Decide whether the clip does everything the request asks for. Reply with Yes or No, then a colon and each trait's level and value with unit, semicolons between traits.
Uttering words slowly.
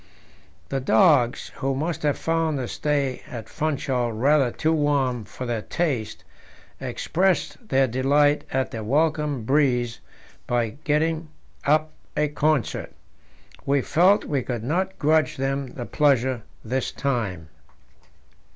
Yes: slow, 125 wpm